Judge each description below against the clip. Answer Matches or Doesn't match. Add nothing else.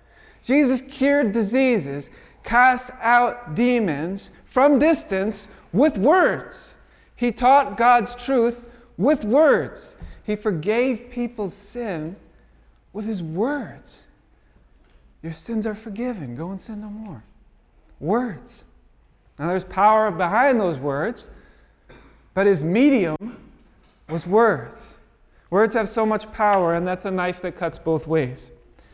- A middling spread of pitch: Doesn't match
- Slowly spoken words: Matches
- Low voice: Doesn't match